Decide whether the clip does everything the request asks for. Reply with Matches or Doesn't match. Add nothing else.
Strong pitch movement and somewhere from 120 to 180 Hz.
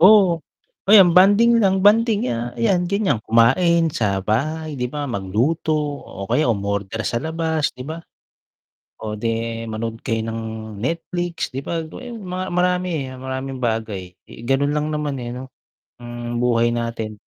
Matches